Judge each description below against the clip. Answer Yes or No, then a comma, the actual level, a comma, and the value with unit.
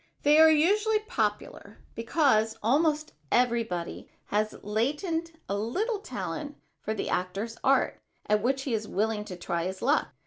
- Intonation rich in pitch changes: Yes, wide, 6.6 semitones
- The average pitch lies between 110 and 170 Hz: No, high, 235 Hz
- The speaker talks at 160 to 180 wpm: No, average, 145 wpm